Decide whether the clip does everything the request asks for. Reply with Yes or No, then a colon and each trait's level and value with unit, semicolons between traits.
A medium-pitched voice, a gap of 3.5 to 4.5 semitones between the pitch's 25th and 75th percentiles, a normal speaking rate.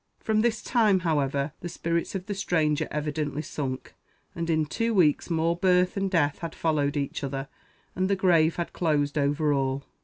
Yes: medium, 160 Hz; average, 4.0 semitones; average, 180 wpm